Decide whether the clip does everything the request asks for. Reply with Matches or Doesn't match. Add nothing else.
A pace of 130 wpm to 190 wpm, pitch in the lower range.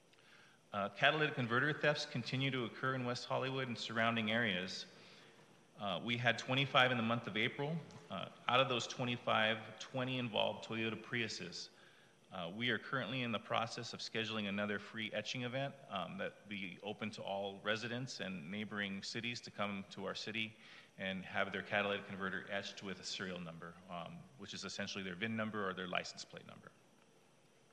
Matches